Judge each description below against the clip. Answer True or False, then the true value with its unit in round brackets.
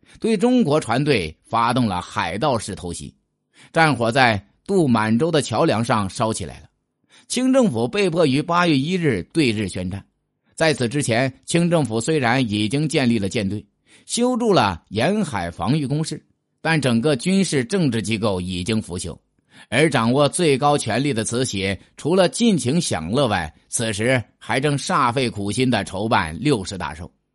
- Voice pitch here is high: False (125 Hz)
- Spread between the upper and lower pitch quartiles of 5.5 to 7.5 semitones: True (6.6 semitones)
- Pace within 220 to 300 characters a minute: True (245 characters per minute)